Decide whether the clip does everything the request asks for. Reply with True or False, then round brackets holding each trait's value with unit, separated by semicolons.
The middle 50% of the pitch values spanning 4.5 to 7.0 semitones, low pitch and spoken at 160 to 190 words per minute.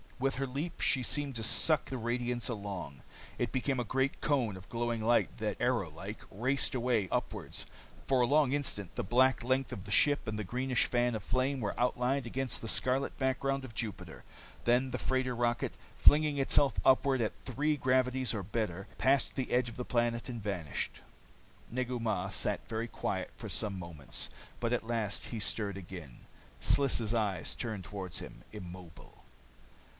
False (3.7 semitones; 120 Hz; 175 wpm)